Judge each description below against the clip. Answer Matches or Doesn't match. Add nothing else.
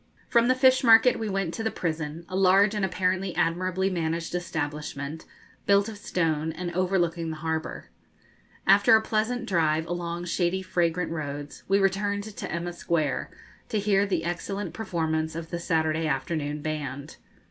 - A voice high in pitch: Doesn't match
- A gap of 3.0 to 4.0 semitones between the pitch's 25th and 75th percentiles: Matches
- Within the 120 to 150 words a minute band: Doesn't match